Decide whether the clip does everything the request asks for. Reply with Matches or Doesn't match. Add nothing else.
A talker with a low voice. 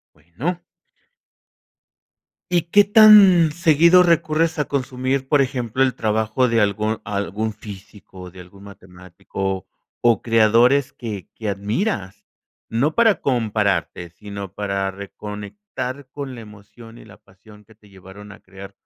Matches